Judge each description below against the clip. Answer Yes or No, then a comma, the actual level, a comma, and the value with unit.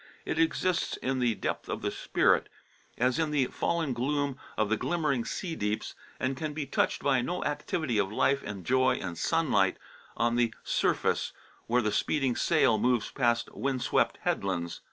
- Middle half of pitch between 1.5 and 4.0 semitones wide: No, average, 4.7 semitones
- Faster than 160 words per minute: Yes, average, 175 wpm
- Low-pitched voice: Yes, low, 130 Hz